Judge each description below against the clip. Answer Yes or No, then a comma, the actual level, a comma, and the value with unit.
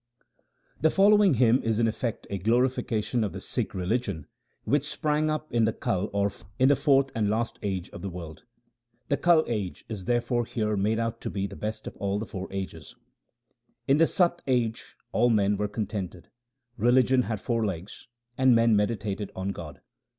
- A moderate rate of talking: Yes, average, 180 wpm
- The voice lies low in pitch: Yes, low, 110 Hz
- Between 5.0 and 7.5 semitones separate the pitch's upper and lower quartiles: No, average, 4.0 semitones